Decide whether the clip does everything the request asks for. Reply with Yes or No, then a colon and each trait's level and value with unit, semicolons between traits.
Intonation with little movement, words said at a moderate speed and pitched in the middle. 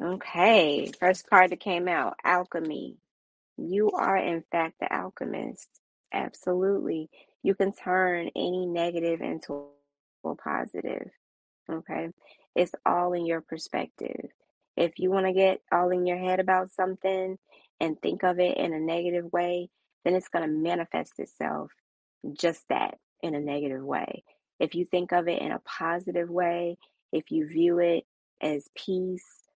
Yes: narrow, 1.8 semitones; average, 150 wpm; medium, 175 Hz